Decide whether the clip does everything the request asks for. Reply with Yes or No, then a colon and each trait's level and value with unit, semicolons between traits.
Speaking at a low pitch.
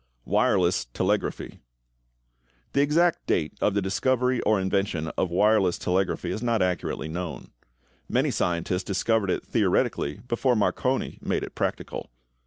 Yes: low, 100 Hz